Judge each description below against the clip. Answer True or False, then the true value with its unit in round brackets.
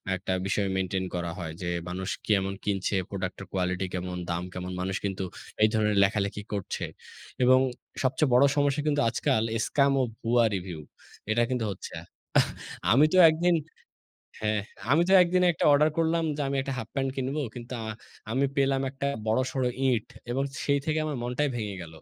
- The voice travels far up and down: True (6.3 semitones)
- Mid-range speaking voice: False (115 Hz)